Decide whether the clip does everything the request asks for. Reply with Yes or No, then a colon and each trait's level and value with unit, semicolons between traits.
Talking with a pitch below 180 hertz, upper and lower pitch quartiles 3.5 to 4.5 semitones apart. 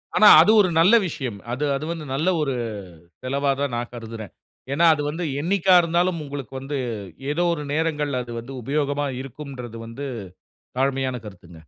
Yes: medium, 140 Hz; average, 4.2 semitones